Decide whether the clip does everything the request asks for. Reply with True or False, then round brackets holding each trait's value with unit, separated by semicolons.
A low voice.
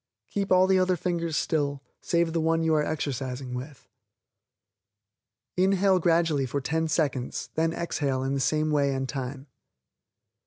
False (155 Hz)